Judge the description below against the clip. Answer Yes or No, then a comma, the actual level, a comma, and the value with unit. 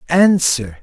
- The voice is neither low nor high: Yes, medium, 155 Hz